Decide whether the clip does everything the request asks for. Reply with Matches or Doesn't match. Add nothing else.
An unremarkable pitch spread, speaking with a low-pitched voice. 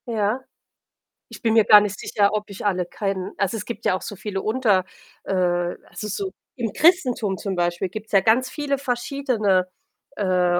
Doesn't match